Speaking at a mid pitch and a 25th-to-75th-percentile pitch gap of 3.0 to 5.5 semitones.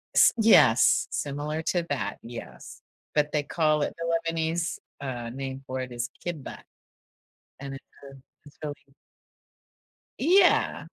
Yes: medium, 145 Hz; average, 3.6 semitones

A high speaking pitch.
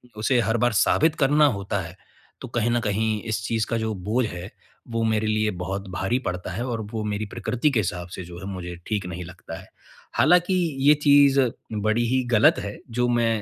No: low, 110 Hz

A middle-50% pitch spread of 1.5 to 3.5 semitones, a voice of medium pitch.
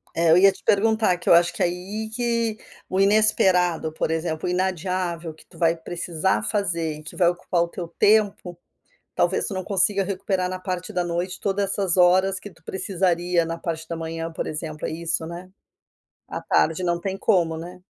Yes: narrow, 2.4 semitones; medium, 180 Hz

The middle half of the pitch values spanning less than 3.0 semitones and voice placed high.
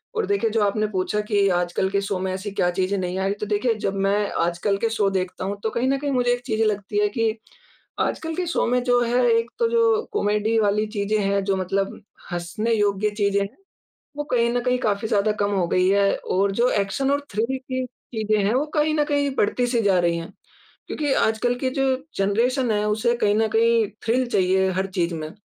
No: average, 3.8 semitones; high, 210 Hz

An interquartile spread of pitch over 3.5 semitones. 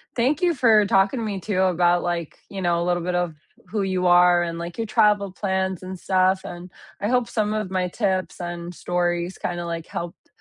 No: average, 2.7 semitones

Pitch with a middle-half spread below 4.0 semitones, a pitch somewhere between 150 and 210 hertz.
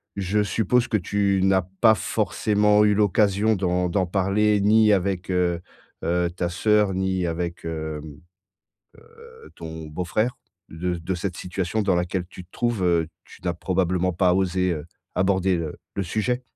No: average, 2.9 semitones; very low, 95 Hz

